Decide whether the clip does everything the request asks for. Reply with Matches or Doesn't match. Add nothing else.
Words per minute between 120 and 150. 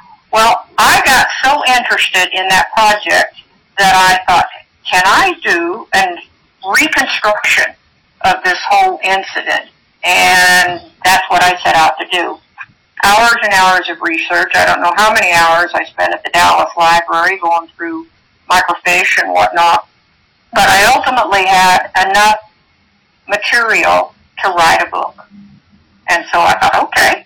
Matches